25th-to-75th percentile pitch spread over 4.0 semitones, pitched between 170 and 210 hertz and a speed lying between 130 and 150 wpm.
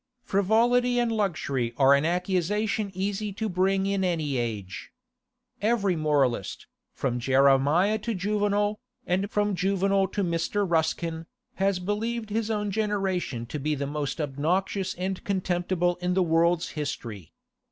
Yes: average, 5.1 semitones; medium, 185 Hz; slow, 135 wpm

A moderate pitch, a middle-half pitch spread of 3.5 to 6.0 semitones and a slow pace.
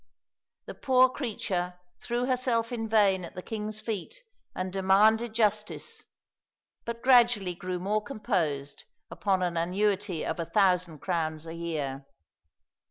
No: high, 200 Hz; average, 4.2 semitones; slow, 130 wpm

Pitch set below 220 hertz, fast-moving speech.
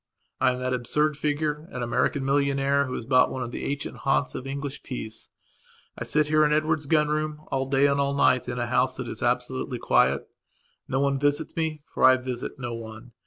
Yes: low, 135 Hz; fast, 215 wpm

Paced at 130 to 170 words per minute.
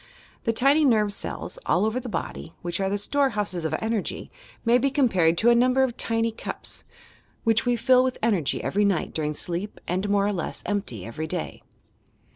No: average, 190 wpm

